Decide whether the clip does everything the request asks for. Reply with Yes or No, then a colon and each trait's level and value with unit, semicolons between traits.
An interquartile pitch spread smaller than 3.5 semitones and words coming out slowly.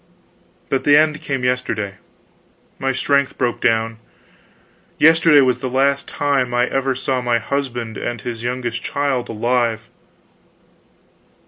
Yes: average, 2.8 semitones; slow, 125 wpm